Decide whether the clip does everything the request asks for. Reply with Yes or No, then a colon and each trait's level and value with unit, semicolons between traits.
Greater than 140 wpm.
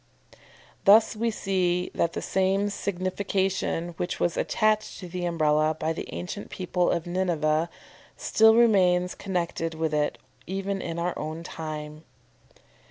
No: slow, 135 wpm